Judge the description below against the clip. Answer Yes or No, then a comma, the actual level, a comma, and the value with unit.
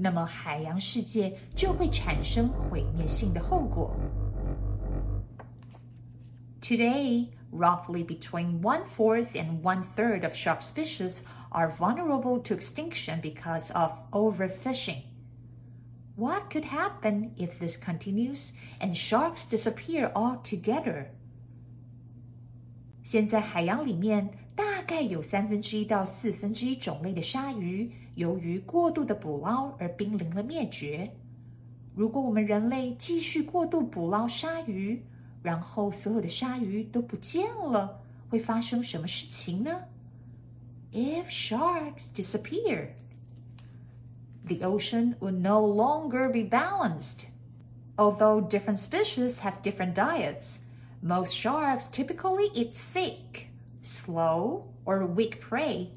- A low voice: No, medium, 185 Hz